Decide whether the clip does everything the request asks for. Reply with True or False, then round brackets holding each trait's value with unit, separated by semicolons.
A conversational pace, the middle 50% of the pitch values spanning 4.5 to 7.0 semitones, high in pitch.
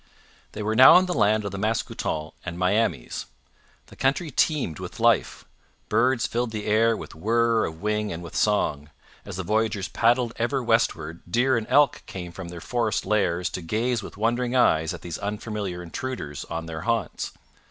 False (180 wpm; 5.1 semitones; 105 Hz)